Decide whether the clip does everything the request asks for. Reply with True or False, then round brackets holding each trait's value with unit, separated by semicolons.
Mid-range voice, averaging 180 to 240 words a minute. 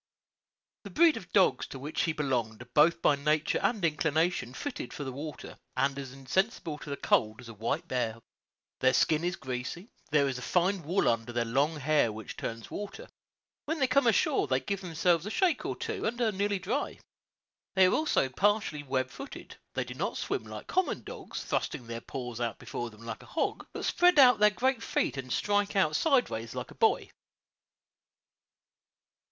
True (155 Hz; 190 wpm)